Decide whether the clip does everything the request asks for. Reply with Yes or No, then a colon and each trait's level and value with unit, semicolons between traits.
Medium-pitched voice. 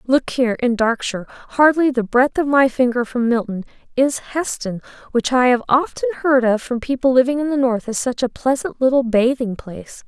No: very high, 250 Hz